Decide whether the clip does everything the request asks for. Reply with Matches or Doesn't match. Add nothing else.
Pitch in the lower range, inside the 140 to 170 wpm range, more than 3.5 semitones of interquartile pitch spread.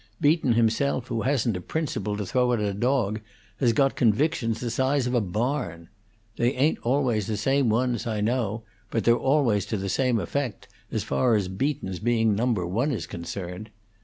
Doesn't match